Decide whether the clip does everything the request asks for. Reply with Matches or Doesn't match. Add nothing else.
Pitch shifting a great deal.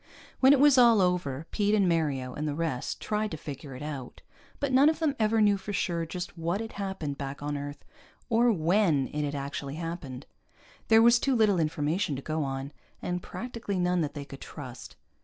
Matches